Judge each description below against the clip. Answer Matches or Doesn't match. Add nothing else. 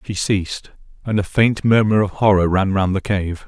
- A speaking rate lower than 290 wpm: Matches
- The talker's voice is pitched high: Doesn't match